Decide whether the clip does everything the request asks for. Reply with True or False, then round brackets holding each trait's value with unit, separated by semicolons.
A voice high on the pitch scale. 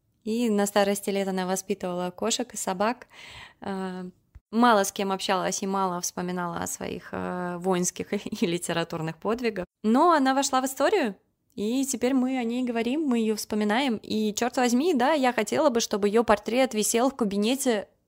True (215 Hz)